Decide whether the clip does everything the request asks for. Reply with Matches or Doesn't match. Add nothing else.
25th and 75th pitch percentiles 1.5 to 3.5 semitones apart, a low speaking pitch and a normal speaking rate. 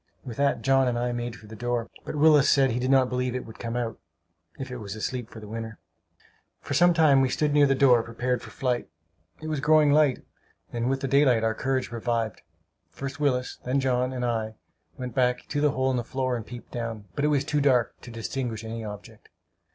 Doesn't match